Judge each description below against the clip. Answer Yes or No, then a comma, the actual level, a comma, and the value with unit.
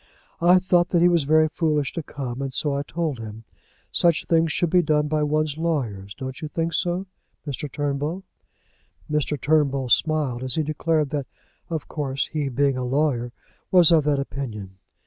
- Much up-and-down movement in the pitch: No, average, 3.2 semitones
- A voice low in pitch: No, medium, 150 Hz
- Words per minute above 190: No, average, 180 wpm